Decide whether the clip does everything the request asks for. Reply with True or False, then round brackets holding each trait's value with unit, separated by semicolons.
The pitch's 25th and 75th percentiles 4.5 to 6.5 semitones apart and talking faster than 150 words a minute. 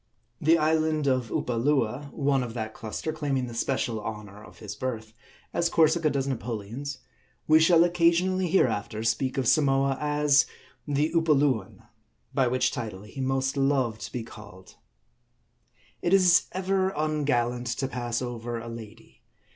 False (4.9 semitones; 145 wpm)